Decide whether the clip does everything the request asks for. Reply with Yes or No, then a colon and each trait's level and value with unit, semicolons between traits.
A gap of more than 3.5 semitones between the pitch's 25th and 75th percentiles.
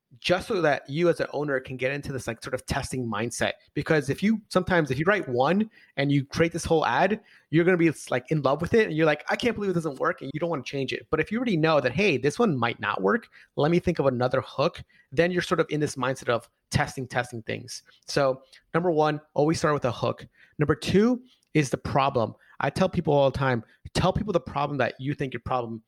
Yes: average, 4.7 semitones